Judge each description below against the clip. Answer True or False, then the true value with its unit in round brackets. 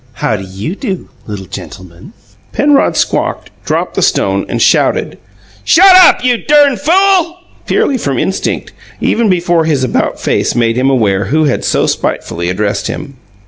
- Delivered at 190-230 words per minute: False (155 wpm)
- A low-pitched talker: False (155 Hz)